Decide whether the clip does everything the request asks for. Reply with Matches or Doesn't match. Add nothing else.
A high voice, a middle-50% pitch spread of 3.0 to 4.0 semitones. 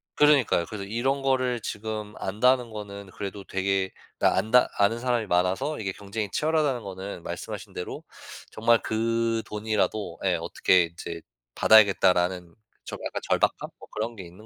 Doesn't match